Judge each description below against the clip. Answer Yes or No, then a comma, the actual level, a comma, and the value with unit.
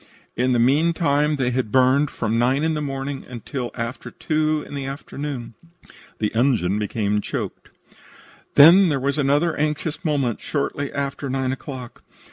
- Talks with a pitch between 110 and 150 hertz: Yes, low, 135 Hz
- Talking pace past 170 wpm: No, average, 155 wpm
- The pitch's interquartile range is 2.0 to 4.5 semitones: Yes, average, 3.1 semitones